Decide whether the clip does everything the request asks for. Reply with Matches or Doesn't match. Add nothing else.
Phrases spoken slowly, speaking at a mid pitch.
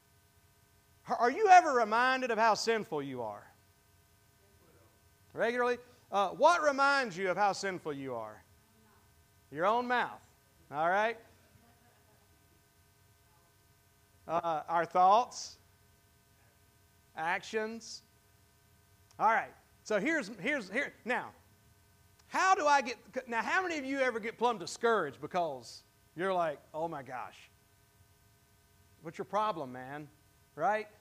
Matches